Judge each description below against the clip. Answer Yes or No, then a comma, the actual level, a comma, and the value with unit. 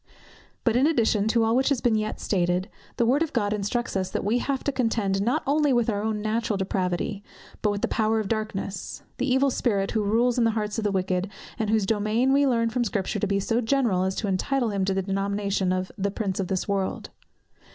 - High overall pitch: Yes, high, 215 Hz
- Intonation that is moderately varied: Yes, average, 3.4 semitones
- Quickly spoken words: Yes, fast, 235 wpm